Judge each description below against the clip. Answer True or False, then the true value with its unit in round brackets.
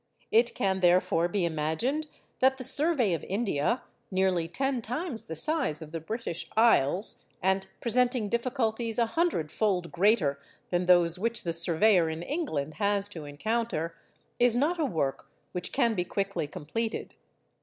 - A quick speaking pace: False (145 wpm)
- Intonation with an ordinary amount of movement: False (6.0 semitones)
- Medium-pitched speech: False (200 Hz)